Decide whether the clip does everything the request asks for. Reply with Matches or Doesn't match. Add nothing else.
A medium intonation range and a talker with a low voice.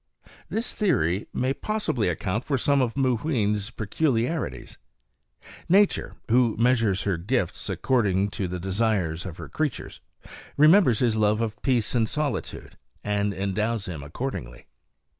Matches